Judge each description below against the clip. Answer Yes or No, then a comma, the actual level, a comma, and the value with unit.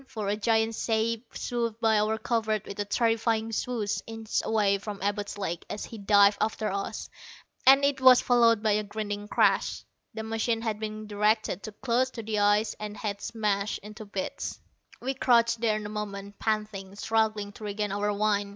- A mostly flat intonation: Yes, narrow, 1.6 semitones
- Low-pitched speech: No, high, 215 Hz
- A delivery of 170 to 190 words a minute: Yes, average, 180 wpm